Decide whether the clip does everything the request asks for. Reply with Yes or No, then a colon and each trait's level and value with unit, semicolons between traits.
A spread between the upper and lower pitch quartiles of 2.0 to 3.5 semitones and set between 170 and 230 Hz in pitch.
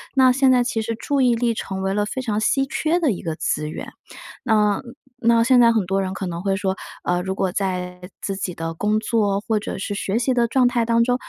No: average, 4.0 semitones; high, 215 Hz